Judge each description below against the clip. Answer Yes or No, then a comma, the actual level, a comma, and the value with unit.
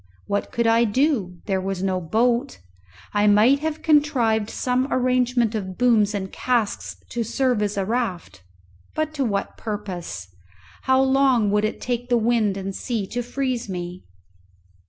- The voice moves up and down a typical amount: Yes, average, 3.9 semitones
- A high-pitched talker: Yes, high, 230 Hz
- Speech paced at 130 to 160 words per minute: Yes, average, 155 wpm